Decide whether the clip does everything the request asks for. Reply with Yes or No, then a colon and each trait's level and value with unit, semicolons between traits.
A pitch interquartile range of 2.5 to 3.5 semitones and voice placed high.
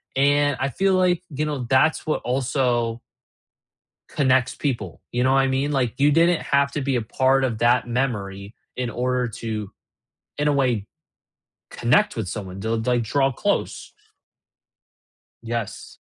No: average, 3.1 semitones; low, 130 Hz